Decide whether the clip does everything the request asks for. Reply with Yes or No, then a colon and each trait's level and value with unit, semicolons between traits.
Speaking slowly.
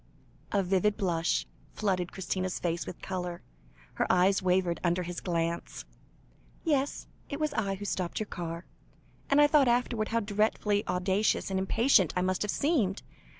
No: average, 155 wpm